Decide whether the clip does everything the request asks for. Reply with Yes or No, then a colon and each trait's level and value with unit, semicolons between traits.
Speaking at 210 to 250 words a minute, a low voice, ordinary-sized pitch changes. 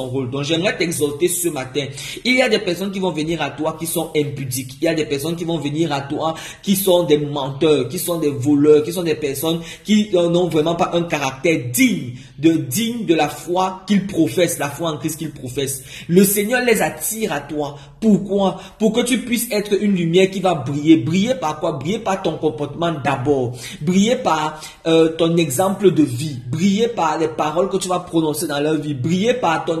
No: average, 215 wpm; medium, 165 Hz; average, 4.0 semitones